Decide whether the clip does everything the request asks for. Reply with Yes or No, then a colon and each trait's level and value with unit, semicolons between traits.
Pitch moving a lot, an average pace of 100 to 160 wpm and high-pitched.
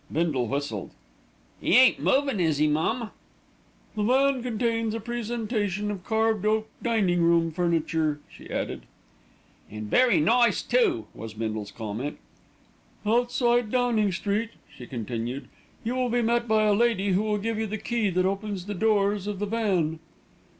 Yes: wide, 5.7 semitones; average, 155 wpm; high, 210 Hz